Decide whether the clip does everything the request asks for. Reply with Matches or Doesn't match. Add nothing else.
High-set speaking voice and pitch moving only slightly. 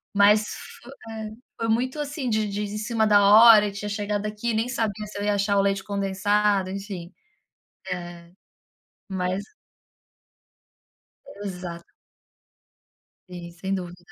Matches